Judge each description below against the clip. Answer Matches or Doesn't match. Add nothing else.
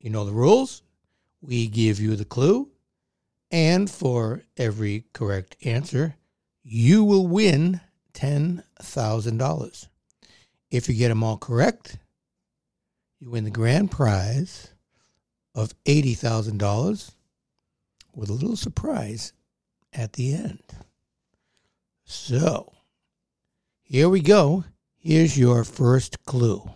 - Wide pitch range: Matches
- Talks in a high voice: Doesn't match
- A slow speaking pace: Matches